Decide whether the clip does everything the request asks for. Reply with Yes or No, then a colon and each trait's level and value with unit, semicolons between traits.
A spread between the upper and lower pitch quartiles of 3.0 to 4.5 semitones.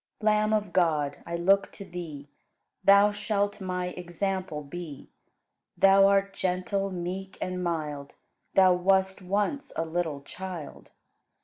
No: narrow, 2.5 semitones